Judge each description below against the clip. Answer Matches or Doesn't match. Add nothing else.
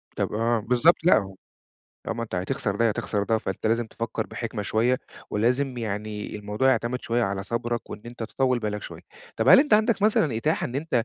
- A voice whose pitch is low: Matches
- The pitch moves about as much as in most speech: Matches